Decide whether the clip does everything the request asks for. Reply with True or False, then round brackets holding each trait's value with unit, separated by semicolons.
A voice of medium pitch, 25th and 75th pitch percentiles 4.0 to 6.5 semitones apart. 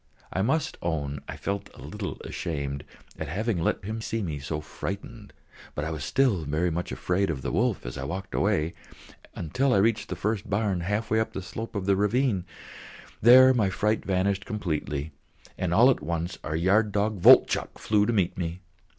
False (95 Hz; 4.8 semitones)